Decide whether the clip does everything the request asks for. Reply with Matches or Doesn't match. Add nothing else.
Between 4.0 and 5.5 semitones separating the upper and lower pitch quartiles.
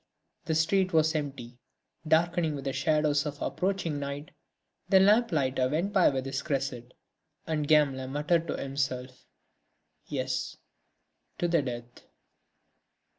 Doesn't match